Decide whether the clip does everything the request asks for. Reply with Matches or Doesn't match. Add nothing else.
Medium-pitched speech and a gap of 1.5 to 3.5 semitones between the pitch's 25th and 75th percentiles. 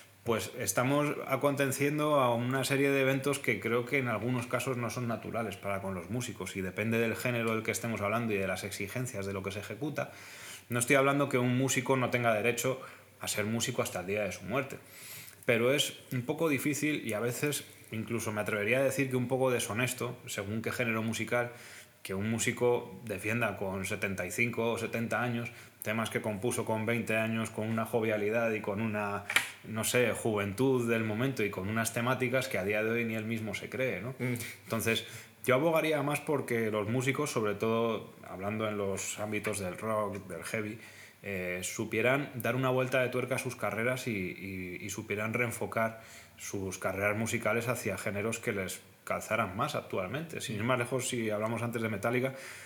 Doesn't match